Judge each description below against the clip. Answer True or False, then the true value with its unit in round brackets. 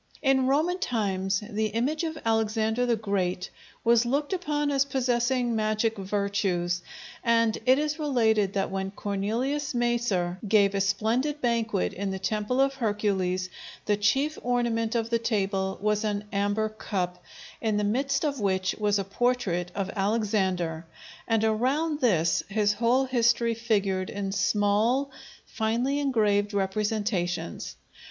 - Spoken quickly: False (140 wpm)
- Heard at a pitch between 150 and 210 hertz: False (220 Hz)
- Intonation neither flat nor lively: True (3.7 semitones)